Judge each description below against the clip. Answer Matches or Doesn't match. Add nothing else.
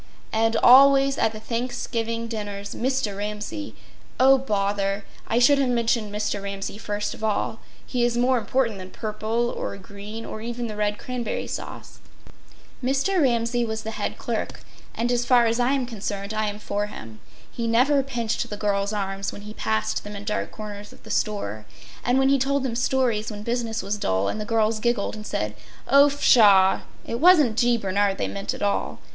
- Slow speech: Doesn't match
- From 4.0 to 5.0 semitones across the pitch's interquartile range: Doesn't match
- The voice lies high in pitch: Matches